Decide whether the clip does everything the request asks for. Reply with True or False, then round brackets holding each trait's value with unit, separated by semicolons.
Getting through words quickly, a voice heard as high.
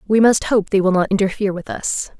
True (245 wpm; 200 Hz)